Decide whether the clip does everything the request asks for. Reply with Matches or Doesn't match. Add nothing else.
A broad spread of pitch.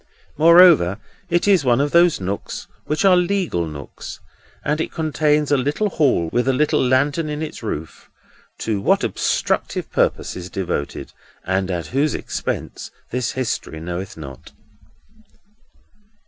Matches